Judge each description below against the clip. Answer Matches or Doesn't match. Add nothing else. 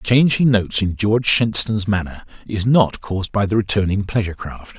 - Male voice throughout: Matches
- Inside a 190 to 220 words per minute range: Matches